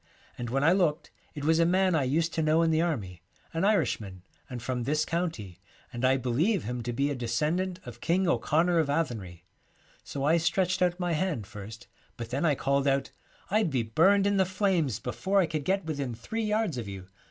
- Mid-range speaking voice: Yes, medium, 155 Hz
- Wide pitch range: Yes, wide, 6.3 semitones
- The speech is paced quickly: Yes, fast, 215 wpm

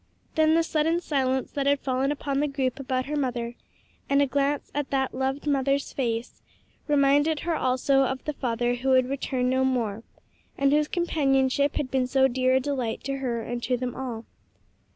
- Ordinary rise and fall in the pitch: No, narrow, 1.8 semitones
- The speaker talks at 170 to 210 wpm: Yes, average, 190 wpm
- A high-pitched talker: Yes, very high, 270 Hz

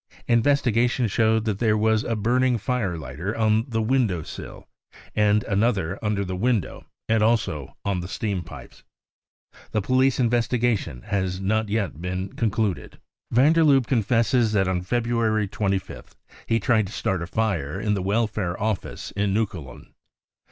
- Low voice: Yes, low, 110 Hz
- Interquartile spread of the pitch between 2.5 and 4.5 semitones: Yes, average, 3.3 semitones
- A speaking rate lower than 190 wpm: Yes, average, 160 wpm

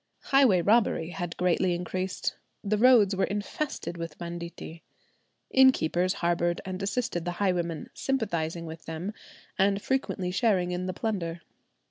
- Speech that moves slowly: Yes, slow, 130 wpm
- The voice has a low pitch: No, medium, 180 Hz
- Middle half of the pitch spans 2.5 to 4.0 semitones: Yes, average, 3.2 semitones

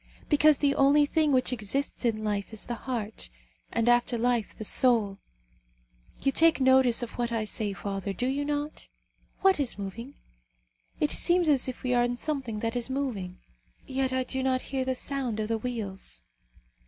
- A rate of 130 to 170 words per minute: No, average, 180 wpm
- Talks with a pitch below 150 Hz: No, very high, 250 Hz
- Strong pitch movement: No, average, 3.8 semitones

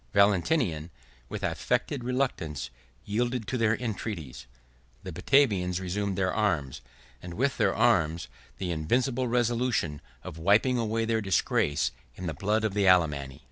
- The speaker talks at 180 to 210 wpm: No, average, 140 wpm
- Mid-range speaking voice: No, low, 100 Hz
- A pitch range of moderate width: No, wide, 6.2 semitones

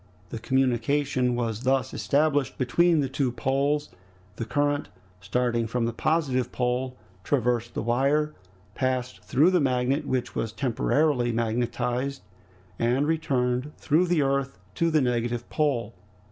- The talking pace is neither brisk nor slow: No, slow, 130 wpm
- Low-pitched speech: Yes, low, 130 Hz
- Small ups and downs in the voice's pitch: No, average, 3.0 semitones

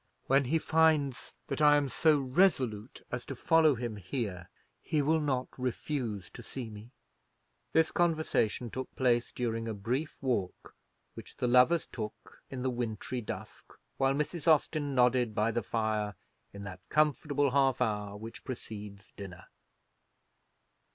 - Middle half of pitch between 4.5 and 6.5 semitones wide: Yes, average, 4.8 semitones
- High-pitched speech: No, low, 125 Hz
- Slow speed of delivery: No, average, 145 wpm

